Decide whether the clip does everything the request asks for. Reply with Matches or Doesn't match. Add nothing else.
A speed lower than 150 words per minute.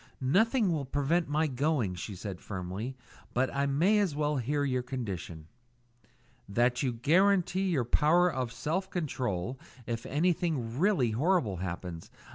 Matches